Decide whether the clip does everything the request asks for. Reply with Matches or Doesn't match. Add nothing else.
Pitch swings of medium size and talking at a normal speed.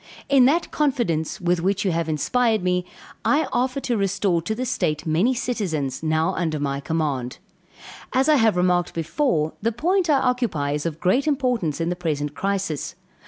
Doesn't match